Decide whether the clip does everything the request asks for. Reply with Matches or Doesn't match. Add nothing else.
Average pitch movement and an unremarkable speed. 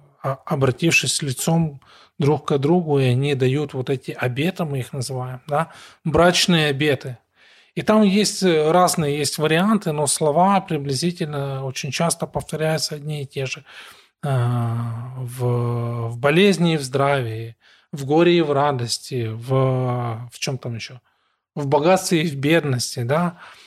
Matches